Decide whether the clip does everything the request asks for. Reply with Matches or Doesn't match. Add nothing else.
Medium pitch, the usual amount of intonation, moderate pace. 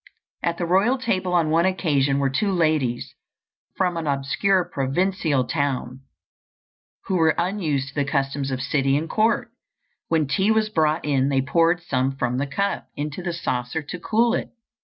Matches